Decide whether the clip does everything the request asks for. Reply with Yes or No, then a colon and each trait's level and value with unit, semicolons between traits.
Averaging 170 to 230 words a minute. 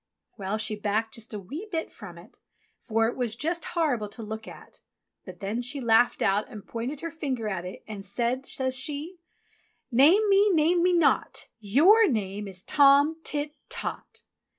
Yes: average, 195 wpm